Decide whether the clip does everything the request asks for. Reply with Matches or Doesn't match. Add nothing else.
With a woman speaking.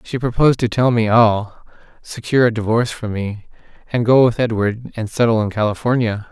Doesn't match